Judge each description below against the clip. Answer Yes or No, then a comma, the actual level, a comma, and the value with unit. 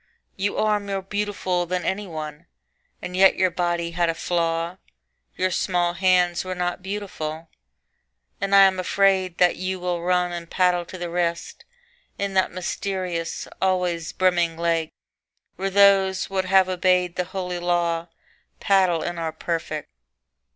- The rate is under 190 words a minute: Yes, average, 150 wpm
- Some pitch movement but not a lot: No, narrow, 1.8 semitones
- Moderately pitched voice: Yes, medium, 180 Hz